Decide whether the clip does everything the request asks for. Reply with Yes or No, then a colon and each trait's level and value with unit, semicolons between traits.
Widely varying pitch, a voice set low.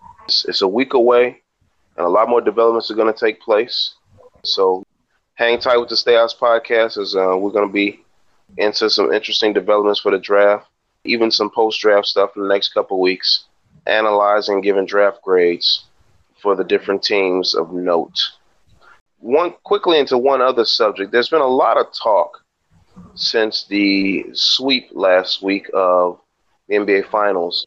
No: average, 3.3 semitones; low, 105 Hz